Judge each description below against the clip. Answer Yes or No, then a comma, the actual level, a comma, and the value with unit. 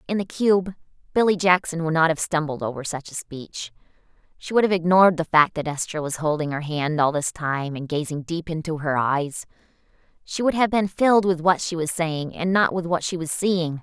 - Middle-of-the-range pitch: Yes, medium, 165 Hz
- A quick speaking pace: Yes, fast, 220 wpm